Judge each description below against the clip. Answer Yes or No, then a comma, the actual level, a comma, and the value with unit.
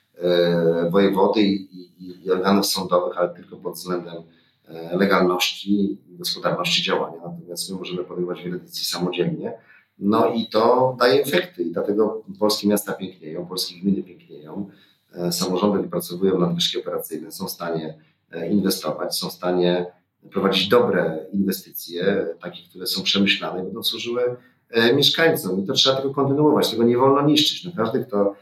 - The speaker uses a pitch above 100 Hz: No, very low, 95 Hz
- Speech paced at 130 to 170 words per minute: Yes, average, 155 wpm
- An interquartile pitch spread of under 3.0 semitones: No, average, 3.7 semitones